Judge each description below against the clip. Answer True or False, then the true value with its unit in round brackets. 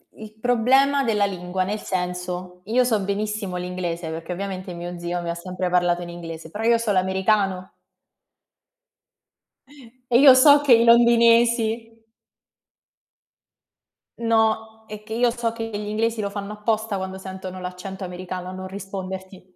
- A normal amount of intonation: True (3.8 semitones)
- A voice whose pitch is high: True (200 Hz)